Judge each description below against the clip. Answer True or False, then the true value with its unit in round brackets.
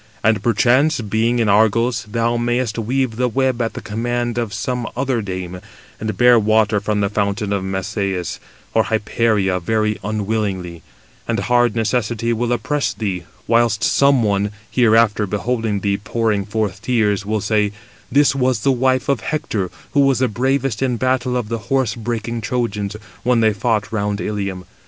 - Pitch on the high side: False (110 Hz)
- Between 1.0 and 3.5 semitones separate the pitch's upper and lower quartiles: True (2.9 semitones)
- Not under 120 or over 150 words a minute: False (165 wpm)